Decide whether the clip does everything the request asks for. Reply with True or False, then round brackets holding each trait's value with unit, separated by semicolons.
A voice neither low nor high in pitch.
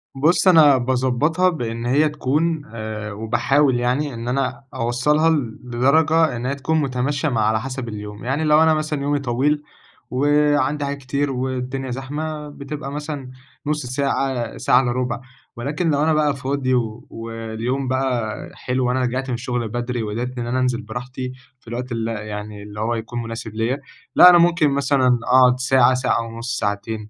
False (130 Hz)